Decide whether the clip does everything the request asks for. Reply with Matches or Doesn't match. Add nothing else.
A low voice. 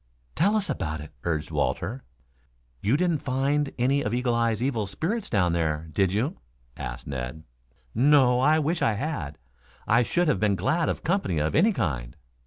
Matches